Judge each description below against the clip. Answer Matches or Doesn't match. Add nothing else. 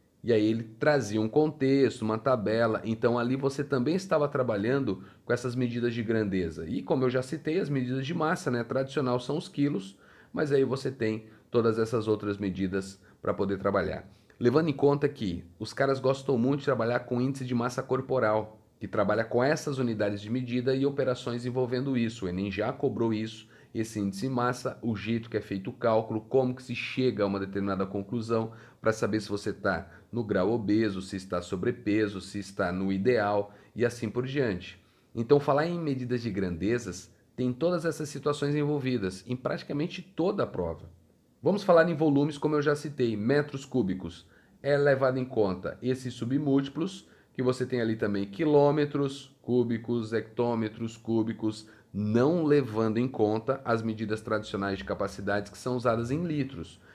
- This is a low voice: Matches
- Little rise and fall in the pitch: Doesn't match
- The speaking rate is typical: Matches